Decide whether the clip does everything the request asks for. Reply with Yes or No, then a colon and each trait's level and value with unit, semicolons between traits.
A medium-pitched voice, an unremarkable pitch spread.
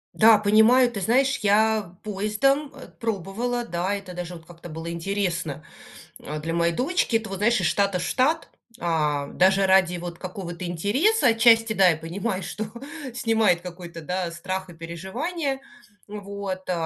No: high, 195 Hz; average, 4.5 semitones